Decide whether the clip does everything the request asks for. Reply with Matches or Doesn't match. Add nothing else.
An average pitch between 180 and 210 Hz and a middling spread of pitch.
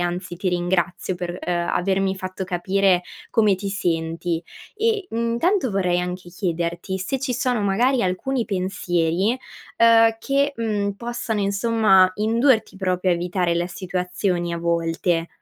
Matches